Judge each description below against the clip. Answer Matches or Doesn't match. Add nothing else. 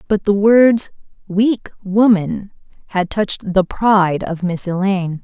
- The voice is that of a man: Doesn't match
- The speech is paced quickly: Doesn't match